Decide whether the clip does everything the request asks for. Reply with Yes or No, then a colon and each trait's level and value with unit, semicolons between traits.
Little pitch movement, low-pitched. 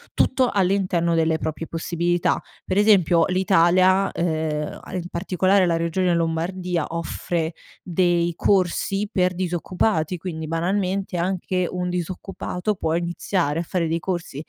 No: narrow, 2.1 semitones; medium, 175 Hz